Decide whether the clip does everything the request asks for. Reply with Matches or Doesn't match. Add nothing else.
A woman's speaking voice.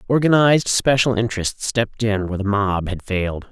Doesn't match